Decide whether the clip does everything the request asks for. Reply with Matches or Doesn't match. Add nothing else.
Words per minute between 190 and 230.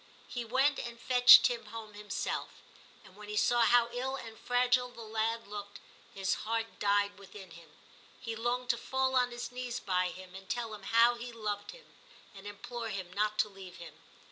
Matches